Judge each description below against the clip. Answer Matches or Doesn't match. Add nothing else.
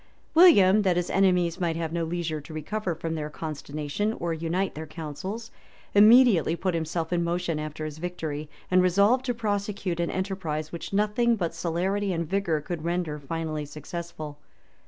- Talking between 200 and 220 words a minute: Doesn't match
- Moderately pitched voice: Matches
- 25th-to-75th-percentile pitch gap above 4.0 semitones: Doesn't match